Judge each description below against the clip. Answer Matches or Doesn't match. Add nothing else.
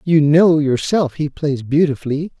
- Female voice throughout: Doesn't match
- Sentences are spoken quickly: Doesn't match